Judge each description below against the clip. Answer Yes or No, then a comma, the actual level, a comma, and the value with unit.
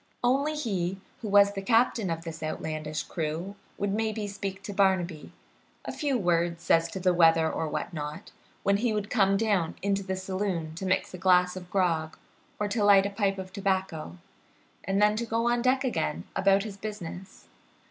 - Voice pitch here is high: Yes, high, 195 Hz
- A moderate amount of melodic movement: Yes, average, 3.3 semitones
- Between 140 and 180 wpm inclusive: No, average, 190 wpm